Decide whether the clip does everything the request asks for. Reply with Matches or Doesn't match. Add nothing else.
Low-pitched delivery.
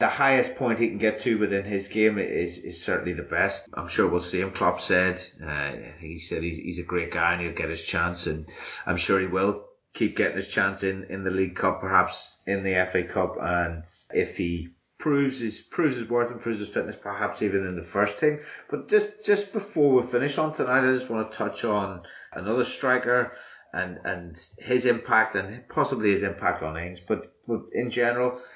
Matches